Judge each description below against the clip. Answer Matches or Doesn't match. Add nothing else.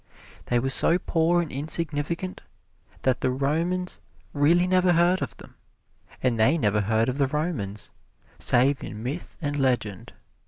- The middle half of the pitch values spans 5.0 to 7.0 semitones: Matches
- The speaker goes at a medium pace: Matches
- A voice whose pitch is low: Doesn't match